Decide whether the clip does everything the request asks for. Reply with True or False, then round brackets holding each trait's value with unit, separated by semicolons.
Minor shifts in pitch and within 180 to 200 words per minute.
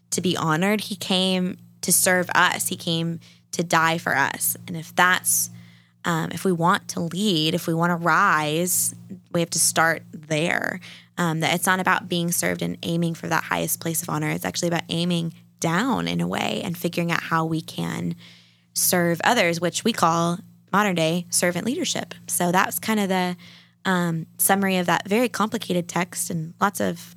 True (2.3 semitones; 190 wpm)